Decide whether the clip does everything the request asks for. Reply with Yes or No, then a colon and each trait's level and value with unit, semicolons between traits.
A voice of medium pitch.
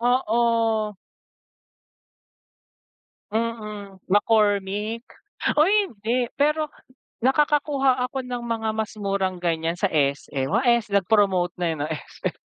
No: high, 220 Hz